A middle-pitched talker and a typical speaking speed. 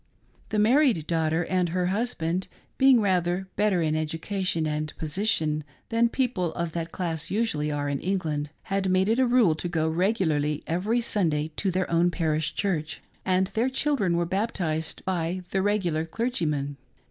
Yes: medium, 180 Hz; average, 160 wpm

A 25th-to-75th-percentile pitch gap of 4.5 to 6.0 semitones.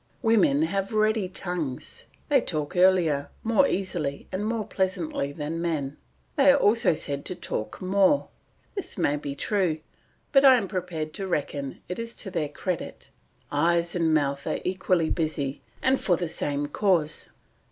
Yes: average, 5.1 semitones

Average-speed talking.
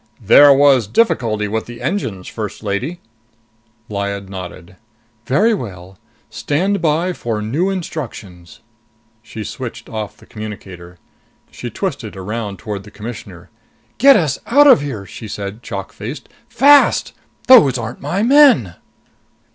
No: slow, 130 wpm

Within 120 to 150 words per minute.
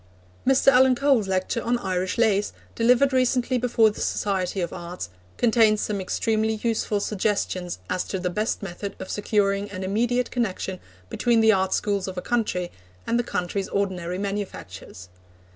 No: average, 160 wpm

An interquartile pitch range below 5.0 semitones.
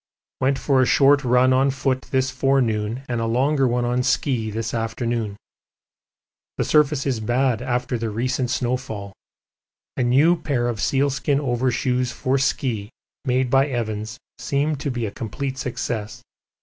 Yes: narrow, 2.4 semitones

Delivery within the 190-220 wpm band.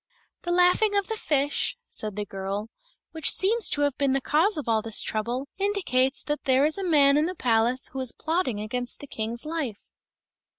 Yes: average, 200 wpm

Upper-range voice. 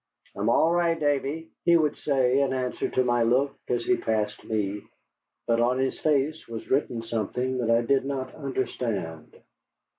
No: low, 130 Hz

